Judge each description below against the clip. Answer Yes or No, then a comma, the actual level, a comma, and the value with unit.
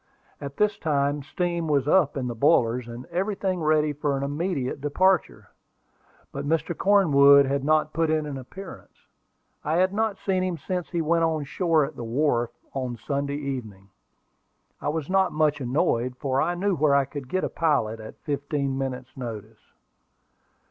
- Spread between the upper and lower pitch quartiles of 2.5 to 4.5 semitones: Yes, average, 3.9 semitones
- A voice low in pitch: No, medium, 145 Hz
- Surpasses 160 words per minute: Yes, average, 170 wpm